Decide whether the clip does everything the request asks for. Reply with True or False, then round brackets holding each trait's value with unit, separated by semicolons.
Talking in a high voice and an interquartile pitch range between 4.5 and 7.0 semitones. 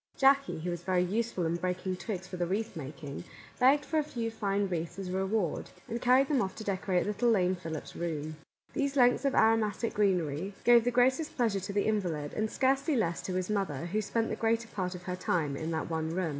True (195 Hz; 4.9 semitones)